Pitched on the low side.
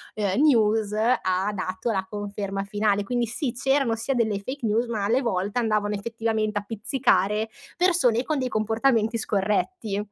No: high, 220 Hz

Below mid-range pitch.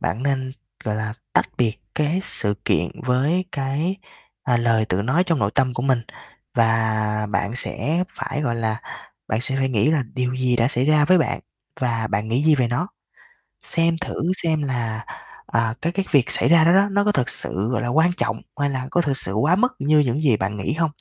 Yes: low, 130 Hz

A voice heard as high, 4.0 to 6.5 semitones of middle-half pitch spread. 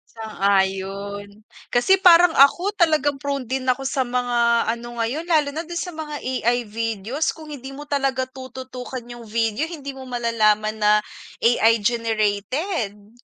Yes: high, 245 Hz; average, 4.4 semitones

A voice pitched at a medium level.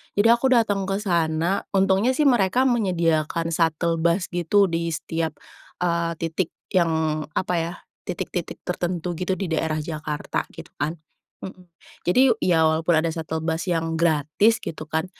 Yes: medium, 170 Hz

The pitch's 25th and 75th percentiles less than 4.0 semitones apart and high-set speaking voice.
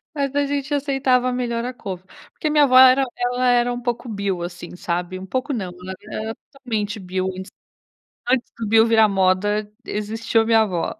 No: average, 4.7 semitones; high, 225 Hz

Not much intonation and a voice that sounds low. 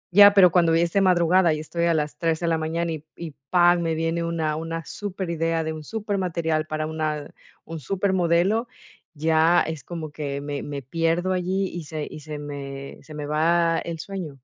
No: narrow, 2.1 semitones; medium, 165 Hz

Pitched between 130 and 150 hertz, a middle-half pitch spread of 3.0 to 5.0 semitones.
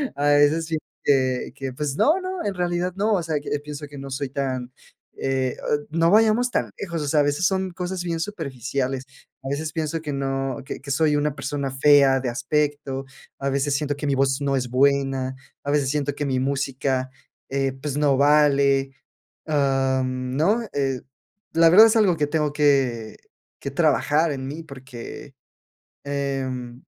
No: medium, 140 Hz; narrow, 2.6 semitones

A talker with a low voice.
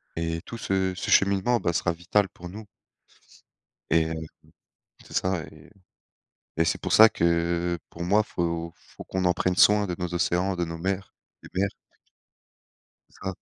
Yes: very low, 90 Hz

